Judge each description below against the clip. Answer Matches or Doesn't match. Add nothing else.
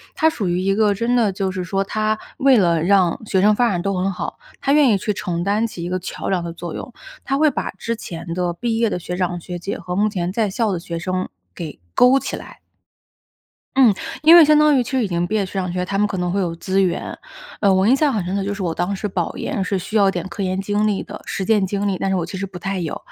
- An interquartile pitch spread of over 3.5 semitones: Doesn't match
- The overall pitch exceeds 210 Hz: Doesn't match